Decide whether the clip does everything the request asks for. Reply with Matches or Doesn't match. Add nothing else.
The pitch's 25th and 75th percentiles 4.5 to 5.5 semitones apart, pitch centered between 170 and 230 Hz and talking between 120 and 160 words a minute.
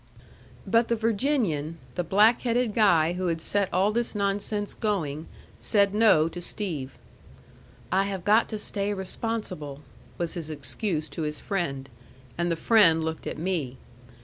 Matches